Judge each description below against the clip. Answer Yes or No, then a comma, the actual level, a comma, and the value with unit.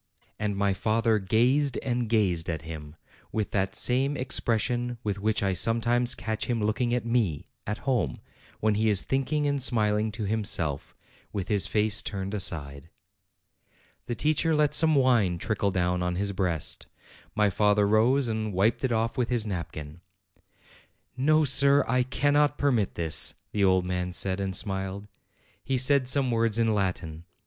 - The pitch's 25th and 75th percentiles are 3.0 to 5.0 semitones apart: Yes, average, 4.4 semitones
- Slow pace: No, average, 165 wpm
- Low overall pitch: Yes, low, 110 Hz